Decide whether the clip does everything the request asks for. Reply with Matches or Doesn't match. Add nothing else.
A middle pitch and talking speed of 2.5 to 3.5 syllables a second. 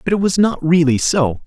Doesn't match